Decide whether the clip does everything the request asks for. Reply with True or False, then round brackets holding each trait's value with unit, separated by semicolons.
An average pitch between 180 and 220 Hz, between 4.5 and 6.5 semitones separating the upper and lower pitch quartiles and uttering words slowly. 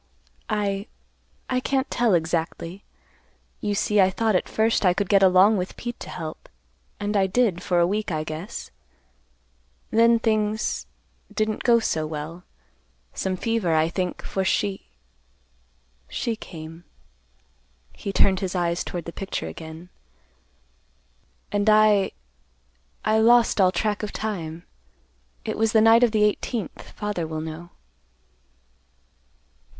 True (190 Hz; 5.0 semitones; 125 wpm)